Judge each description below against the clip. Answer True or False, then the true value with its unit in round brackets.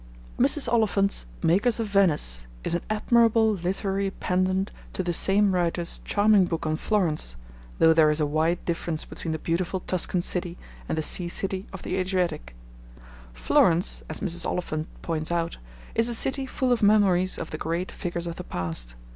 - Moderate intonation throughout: True (3.4 semitones)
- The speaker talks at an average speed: True (170 wpm)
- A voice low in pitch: False (180 Hz)